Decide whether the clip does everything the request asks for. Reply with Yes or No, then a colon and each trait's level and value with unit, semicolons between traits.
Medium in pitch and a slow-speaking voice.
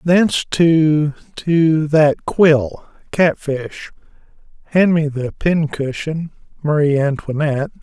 Yes: medium, 150 Hz; slow, 70 wpm